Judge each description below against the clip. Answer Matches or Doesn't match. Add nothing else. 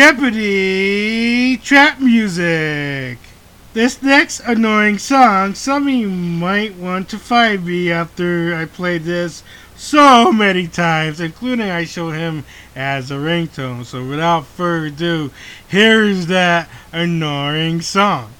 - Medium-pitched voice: Matches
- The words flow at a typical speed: Doesn't match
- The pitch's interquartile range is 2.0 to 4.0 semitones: Doesn't match